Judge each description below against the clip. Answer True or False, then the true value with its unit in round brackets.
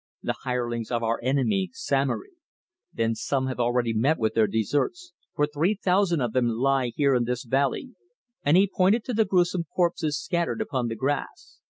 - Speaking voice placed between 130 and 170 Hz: True (135 Hz)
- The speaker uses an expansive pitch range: True (7.0 semitones)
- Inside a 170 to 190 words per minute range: True (180 wpm)